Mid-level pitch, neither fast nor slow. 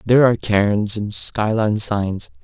No: low, 105 Hz; average, 150 wpm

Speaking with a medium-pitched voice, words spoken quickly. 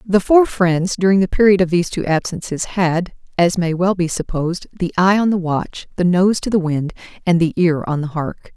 Yes: medium, 180 Hz; fast, 225 wpm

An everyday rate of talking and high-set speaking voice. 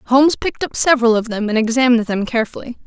No: fast, 210 wpm; high, 240 Hz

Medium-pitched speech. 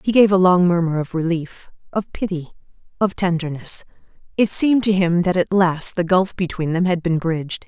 Yes: medium, 175 Hz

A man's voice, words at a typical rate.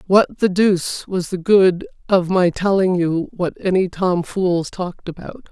No: female; average, 175 wpm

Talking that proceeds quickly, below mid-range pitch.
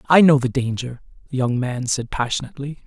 No: average, 190 wpm; low, 130 Hz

